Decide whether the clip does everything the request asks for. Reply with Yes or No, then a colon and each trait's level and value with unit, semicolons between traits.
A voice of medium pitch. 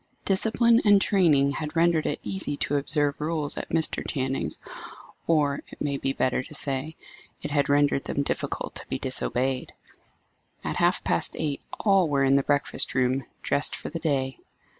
Yes: medium, 145 Hz